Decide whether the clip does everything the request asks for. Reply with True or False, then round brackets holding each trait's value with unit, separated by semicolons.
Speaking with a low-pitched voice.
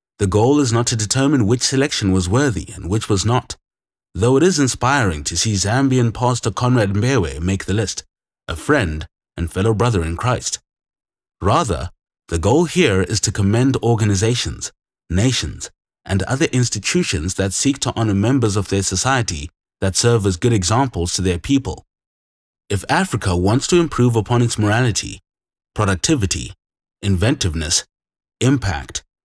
True (105 Hz)